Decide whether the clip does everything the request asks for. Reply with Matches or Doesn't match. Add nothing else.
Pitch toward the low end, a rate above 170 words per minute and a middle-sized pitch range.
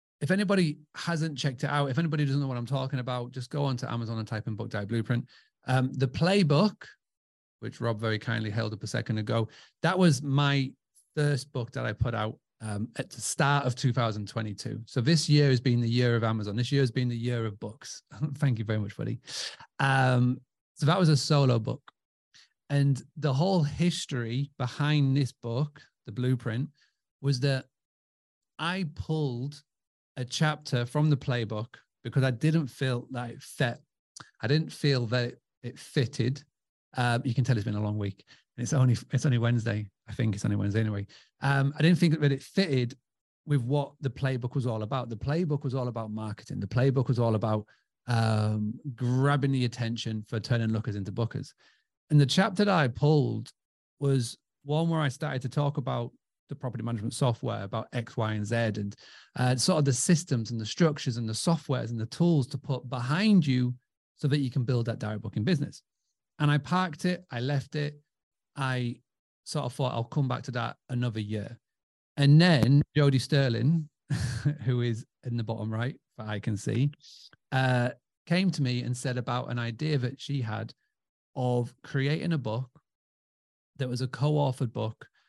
Matches